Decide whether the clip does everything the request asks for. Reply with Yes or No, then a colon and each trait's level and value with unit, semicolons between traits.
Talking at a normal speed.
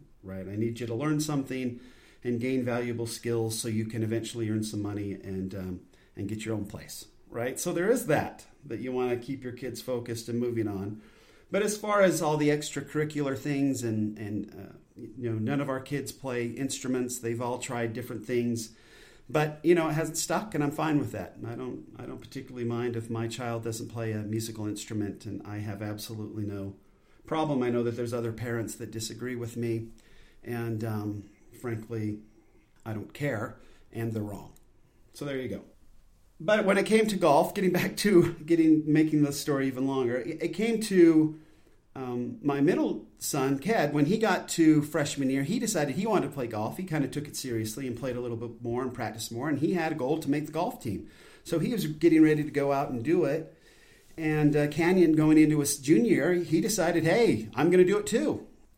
No: fast, 210 wpm